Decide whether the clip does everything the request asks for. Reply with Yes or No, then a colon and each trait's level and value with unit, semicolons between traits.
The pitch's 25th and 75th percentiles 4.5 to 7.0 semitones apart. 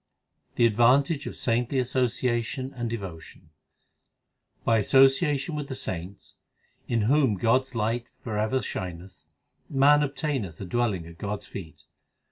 Yes: average, 5.0 semitones